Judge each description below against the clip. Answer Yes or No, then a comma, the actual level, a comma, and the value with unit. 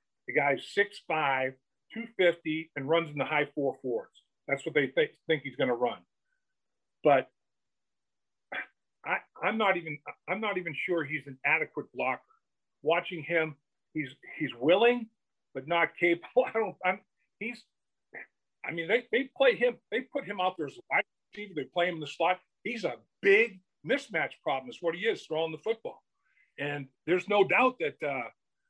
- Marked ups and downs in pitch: Yes, wide, 7.1 semitones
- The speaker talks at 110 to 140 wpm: No, average, 170 wpm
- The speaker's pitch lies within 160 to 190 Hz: Yes, medium, 185 Hz